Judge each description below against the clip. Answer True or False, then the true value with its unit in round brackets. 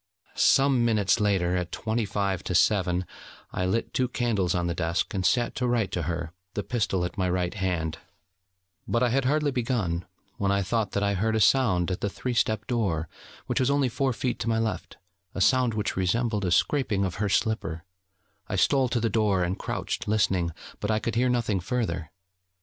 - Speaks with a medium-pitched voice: False (105 Hz)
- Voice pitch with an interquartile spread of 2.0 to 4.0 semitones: False (4.6 semitones)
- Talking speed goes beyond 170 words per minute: True (200 wpm)